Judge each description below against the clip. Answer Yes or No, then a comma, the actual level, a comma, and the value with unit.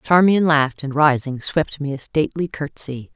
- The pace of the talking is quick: No, average, 170 wpm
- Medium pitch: Yes, medium, 145 Hz